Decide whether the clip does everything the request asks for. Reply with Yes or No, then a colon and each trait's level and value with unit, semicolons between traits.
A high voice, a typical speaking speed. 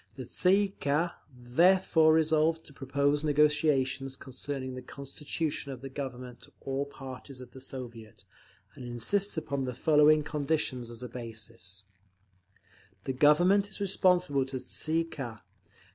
No: medium, 140 Hz; average, 150 wpm